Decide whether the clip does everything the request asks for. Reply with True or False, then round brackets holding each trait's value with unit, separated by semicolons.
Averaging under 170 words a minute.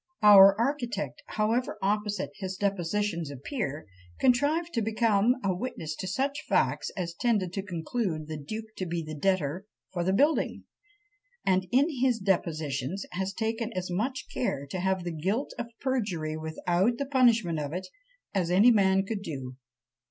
True (160 wpm)